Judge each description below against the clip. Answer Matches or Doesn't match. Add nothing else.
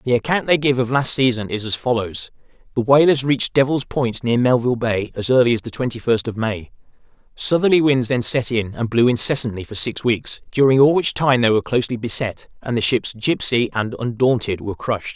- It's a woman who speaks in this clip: Doesn't match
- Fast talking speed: Matches